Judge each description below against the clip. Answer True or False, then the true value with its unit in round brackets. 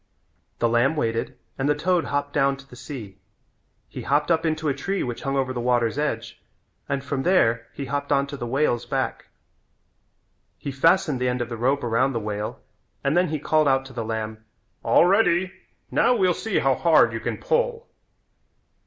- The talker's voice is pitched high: False (135 Hz)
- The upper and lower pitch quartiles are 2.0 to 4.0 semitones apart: False (4.4 semitones)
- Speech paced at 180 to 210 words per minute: True (195 wpm)